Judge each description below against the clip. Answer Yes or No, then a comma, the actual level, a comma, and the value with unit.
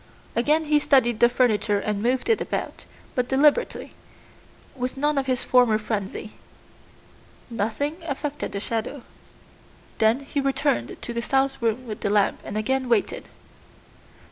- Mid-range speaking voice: No, very high, 250 Hz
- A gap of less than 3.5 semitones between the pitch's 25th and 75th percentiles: No, average, 4.0 semitones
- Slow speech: No, average, 145 wpm